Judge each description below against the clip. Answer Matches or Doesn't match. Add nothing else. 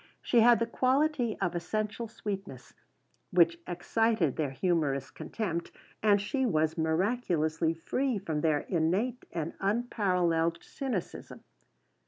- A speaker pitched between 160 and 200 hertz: Matches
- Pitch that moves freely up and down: Matches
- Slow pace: Matches